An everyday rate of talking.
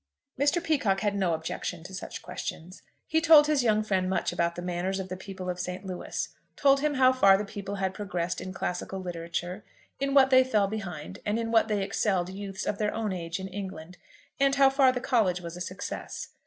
No: fast, 215 wpm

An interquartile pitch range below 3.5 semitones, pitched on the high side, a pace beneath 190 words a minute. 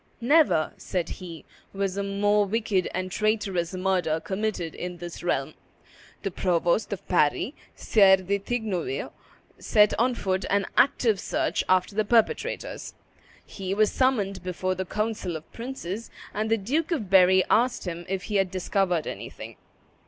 Yes: average, 3.0 semitones; high, 195 Hz; average, 150 wpm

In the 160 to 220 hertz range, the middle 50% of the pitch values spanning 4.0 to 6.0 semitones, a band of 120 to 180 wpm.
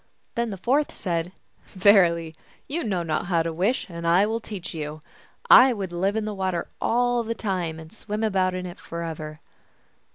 No: medium, 185 Hz; average, 4.4 semitones; average, 190 wpm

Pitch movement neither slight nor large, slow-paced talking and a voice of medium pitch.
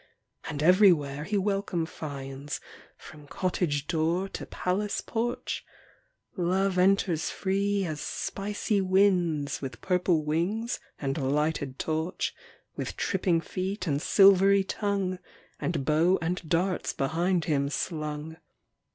Yes: average, 4.2 semitones; slow, 115 wpm; medium, 175 Hz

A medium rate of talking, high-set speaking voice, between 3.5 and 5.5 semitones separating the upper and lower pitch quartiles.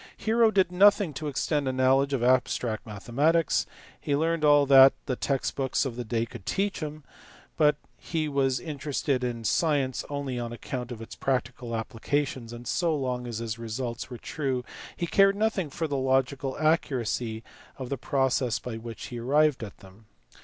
No: average, 180 wpm; low, 135 Hz; average, 3.8 semitones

